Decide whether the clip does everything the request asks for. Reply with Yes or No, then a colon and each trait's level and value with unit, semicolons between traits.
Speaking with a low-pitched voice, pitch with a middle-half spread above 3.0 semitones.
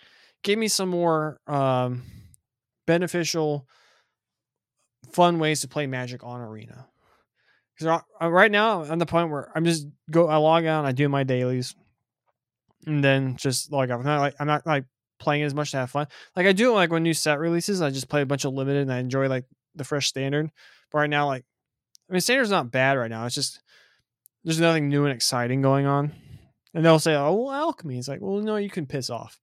No: medium, 145 Hz; average, 3.8 semitones